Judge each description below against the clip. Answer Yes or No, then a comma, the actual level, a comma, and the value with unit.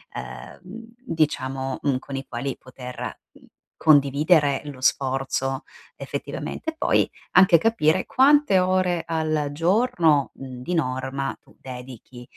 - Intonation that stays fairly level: No, average, 4.4 semitones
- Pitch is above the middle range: No, medium, 140 Hz